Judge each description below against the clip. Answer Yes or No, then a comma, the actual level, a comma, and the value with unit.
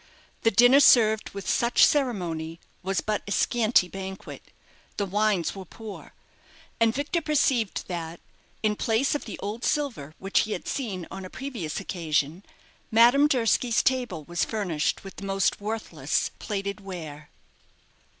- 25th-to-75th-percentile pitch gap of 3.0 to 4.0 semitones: No, average, 4.7 semitones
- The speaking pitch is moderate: No, high, 205 Hz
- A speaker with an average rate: Yes, average, 145 wpm